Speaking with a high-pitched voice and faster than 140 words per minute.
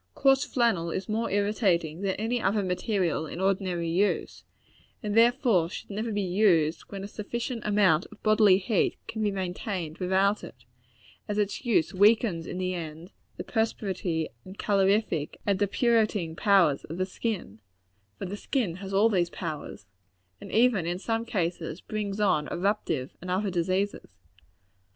Yes: high, 195 Hz; average, 155 wpm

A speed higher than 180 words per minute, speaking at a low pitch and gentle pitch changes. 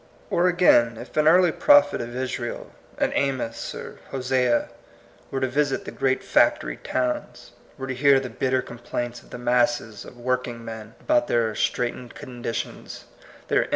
No: average, 165 wpm; low, 125 Hz; narrow, 2.3 semitones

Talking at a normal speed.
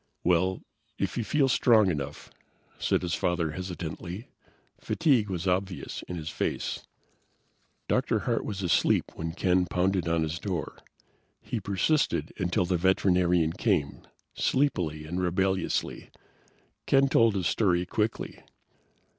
No: slow, 125 wpm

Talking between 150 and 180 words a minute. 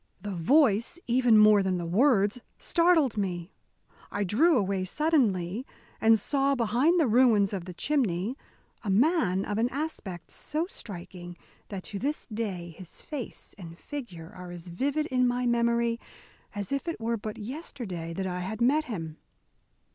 Yes: average, 160 wpm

